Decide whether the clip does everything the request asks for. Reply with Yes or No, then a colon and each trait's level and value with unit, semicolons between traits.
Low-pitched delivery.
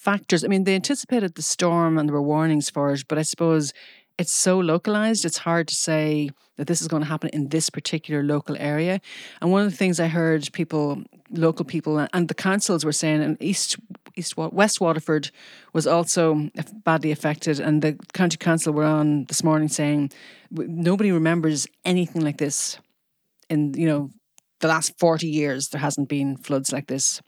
No: medium, 160 Hz